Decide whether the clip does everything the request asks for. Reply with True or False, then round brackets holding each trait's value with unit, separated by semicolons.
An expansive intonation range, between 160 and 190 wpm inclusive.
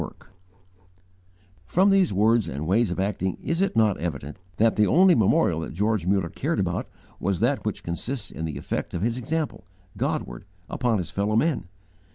True (5.9 semitones; 180 wpm)